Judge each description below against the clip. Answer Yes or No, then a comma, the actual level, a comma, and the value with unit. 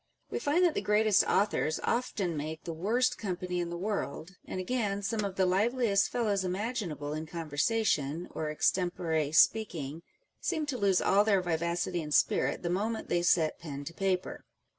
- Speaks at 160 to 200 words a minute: Yes, average, 175 wpm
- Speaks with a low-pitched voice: No, medium, 185 Hz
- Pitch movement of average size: Yes, average, 4.6 semitones